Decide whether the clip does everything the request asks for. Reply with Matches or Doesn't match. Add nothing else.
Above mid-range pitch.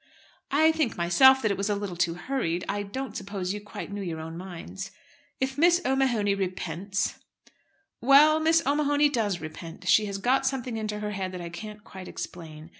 Matches